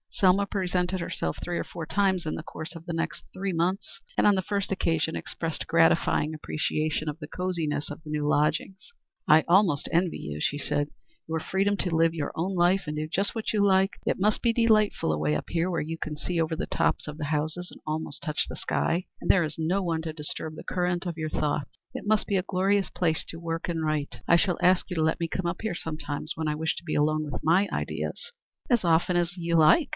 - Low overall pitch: No, medium, 165 Hz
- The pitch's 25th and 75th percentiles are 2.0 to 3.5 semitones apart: Yes, average, 3.2 semitones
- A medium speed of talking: No, fast, 240 wpm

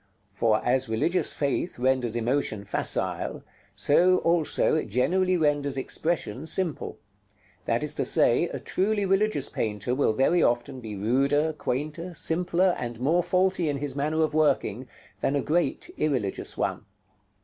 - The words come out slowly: No, average, 145 wpm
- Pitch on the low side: No, medium, 145 Hz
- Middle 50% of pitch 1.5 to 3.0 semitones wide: No, wide, 5.6 semitones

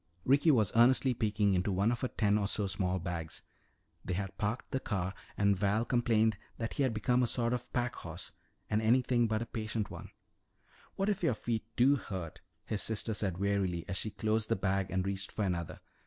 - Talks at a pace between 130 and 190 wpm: No, average, 200 wpm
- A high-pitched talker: No, low, 110 Hz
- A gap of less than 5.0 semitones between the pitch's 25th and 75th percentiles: Yes, average, 3.6 semitones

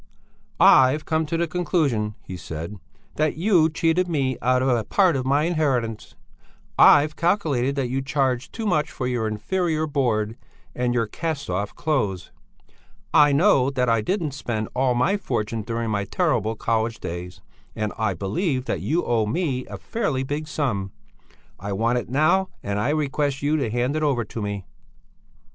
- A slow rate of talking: No, average, 170 wpm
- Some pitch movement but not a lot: No, wide, 5.7 semitones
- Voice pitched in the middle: No, low, 130 Hz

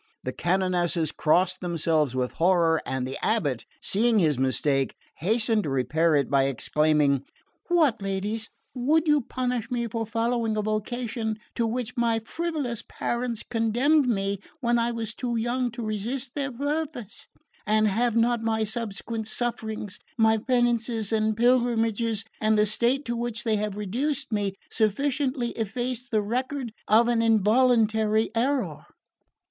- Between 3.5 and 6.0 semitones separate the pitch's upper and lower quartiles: No, average, 3.1 semitones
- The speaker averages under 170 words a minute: Yes, average, 145 wpm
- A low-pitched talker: No, high, 225 Hz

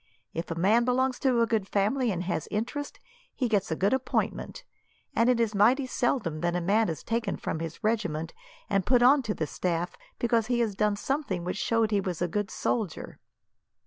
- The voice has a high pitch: Yes, high, 210 Hz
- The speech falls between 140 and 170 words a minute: No, fast, 205 wpm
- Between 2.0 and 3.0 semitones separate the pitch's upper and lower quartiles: No, average, 5.1 semitones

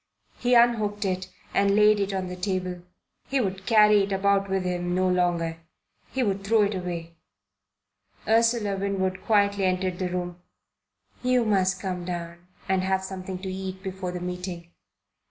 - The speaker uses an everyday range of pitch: No, narrow, 1.9 semitones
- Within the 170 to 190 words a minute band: No, average, 160 wpm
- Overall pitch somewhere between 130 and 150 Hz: No, high, 190 Hz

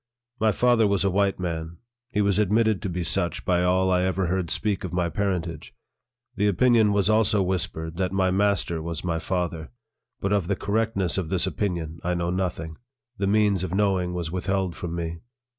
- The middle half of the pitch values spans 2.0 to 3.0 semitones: Yes, average, 2.7 semitones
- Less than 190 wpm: No, average, 195 wpm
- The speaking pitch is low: Yes, very low, 95 Hz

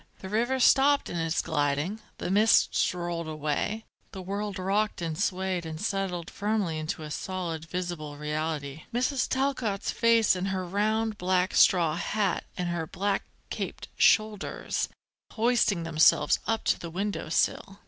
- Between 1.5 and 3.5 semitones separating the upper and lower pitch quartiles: No, average, 4.4 semitones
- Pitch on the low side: No, medium, 185 Hz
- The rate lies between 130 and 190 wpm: Yes, average, 150 wpm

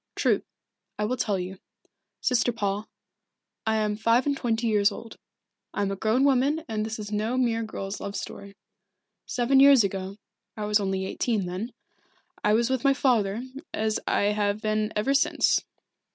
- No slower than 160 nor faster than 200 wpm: Yes, average, 170 wpm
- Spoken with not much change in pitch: No, average, 3.1 semitones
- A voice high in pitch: Yes, high, 215 Hz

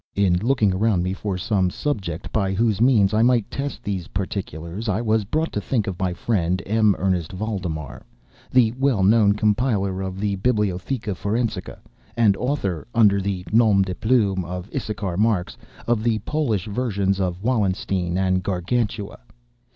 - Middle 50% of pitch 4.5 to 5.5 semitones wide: No, average, 3.3 semitones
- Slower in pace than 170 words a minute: Yes, average, 160 wpm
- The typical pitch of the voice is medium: No, low, 100 Hz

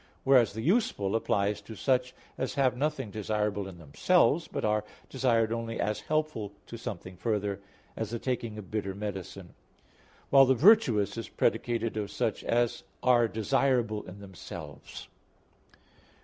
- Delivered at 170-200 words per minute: No, average, 145 wpm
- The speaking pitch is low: Yes, low, 110 Hz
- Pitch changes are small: No, average, 3.8 semitones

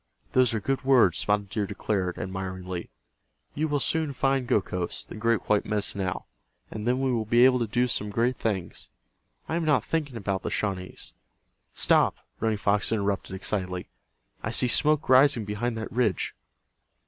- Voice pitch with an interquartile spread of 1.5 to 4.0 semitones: No, average, 4.5 semitones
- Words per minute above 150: Yes, average, 170 wpm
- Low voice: Yes, low, 110 Hz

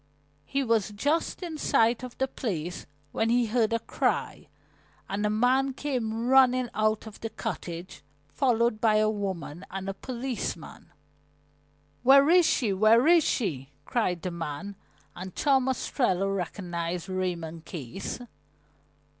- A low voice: No, high, 215 Hz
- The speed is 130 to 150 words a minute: Yes, average, 140 wpm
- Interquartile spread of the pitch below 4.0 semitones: No, wide, 5.4 semitones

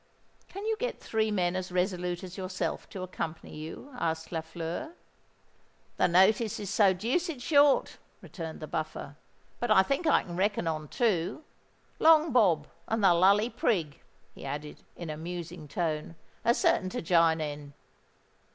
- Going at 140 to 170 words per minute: Yes, average, 155 wpm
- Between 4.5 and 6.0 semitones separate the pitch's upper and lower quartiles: Yes, average, 5.2 semitones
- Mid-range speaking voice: Yes, medium, 180 Hz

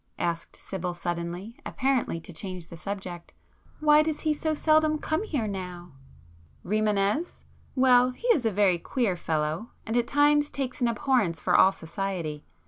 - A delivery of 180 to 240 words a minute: No, average, 150 wpm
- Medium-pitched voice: No, high, 210 Hz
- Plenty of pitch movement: Yes, wide, 7.7 semitones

